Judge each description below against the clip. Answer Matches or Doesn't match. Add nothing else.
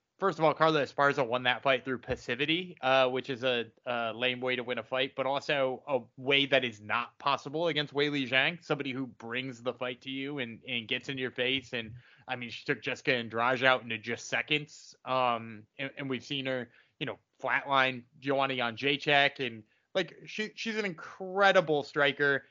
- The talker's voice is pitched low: Matches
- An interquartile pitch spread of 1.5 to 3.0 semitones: Matches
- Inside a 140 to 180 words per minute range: Doesn't match